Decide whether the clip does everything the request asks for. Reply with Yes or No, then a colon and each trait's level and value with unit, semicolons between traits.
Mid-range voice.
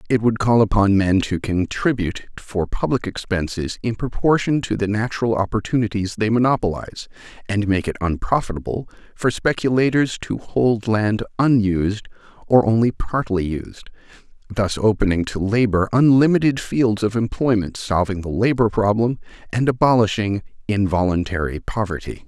No: low, 110 Hz